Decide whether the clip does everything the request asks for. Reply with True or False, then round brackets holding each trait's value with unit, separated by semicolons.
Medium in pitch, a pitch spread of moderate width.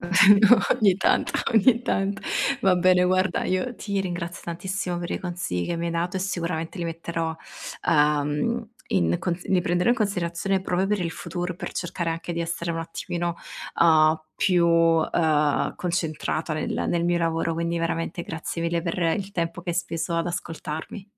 False (170 Hz; 2.0 semitones)